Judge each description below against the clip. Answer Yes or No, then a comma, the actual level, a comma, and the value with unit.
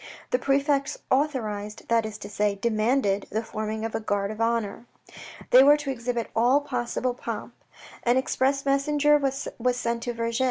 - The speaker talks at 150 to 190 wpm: Yes, average, 165 wpm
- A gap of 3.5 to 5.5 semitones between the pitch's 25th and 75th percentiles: Yes, average, 4.0 semitones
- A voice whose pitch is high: Yes, high, 240 Hz